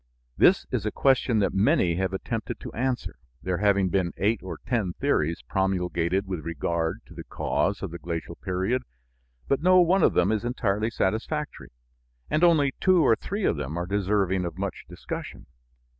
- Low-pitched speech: Yes, low, 100 Hz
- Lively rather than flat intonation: Yes, wide, 5.7 semitones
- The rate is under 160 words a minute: No, average, 175 wpm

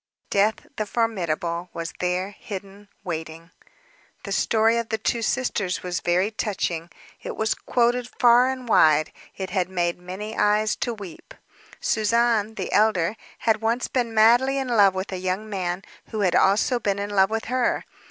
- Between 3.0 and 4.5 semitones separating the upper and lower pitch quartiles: Yes, average, 3.7 semitones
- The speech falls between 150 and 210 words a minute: Yes, average, 165 wpm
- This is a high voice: Yes, high, 205 Hz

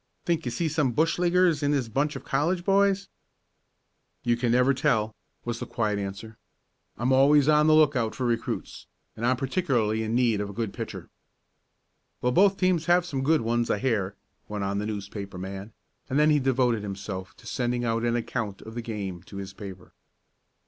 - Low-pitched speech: Yes, low, 120 Hz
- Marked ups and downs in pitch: Yes, wide, 5.8 semitones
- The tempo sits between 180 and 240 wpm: Yes, average, 190 wpm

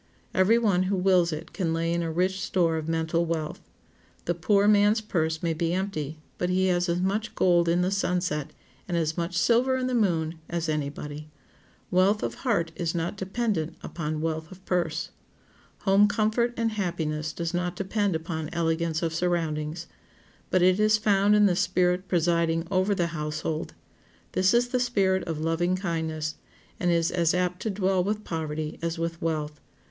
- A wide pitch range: No, average, 3.0 semitones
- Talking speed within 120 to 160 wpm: No, average, 180 wpm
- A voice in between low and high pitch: Yes, medium, 175 Hz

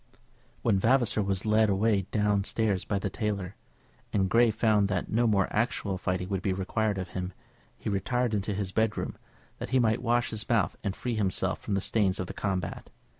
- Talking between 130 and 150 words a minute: No, average, 195 wpm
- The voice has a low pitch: Yes, low, 105 Hz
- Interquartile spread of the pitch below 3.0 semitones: Yes, narrow, 2.5 semitones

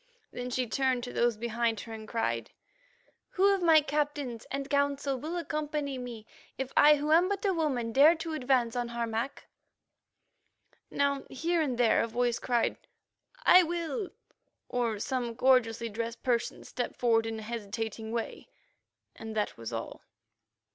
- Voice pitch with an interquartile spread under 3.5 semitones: No, average, 4.3 semitones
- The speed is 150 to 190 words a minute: Yes, average, 155 wpm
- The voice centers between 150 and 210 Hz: No, very high, 250 Hz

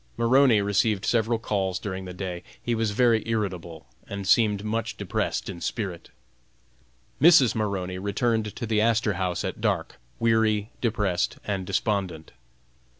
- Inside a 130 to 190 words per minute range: Yes, average, 140 wpm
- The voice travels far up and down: No, average, 3.2 semitones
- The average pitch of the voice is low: Yes, low, 105 Hz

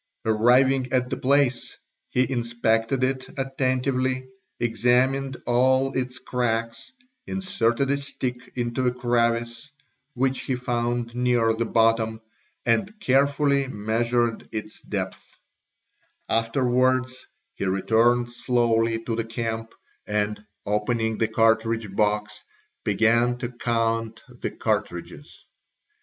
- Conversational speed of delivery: No, slow, 105 wpm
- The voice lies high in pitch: No, low, 120 Hz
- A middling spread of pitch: No, narrow, 2.2 semitones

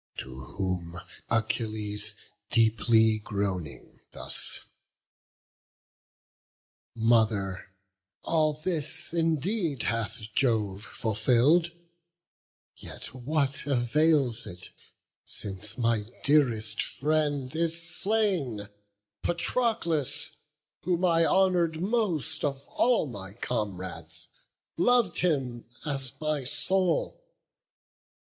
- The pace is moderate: No, slow, 80 wpm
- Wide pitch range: Yes, wide, 7.2 semitones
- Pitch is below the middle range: Yes, low, 130 Hz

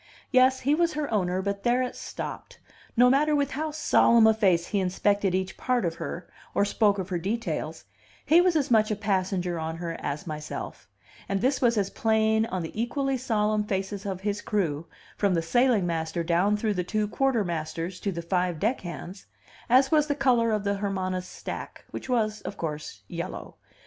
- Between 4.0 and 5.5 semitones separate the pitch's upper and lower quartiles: Yes, average, 5.1 semitones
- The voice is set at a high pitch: Yes, high, 205 Hz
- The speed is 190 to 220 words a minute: Yes, average, 195 wpm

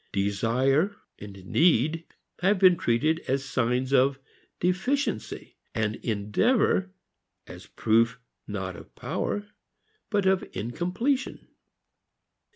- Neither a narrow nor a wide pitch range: No, wide, 8.7 semitones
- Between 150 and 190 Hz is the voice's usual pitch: No, low, 135 Hz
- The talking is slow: Yes, slow, 95 wpm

